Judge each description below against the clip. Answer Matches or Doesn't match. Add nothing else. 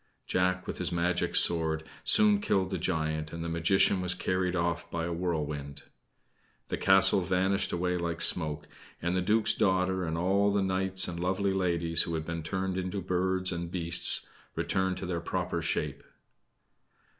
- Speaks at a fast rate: Doesn't match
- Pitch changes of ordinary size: Doesn't match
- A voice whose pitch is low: Matches